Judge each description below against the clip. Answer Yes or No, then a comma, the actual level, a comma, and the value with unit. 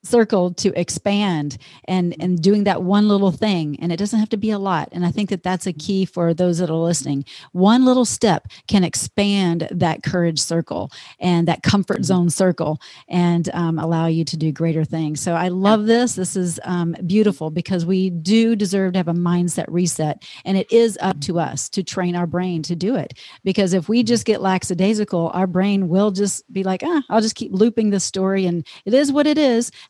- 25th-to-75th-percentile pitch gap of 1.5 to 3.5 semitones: Yes, average, 3.1 semitones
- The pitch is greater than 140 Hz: Yes, medium, 185 Hz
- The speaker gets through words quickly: Yes, fast, 215 wpm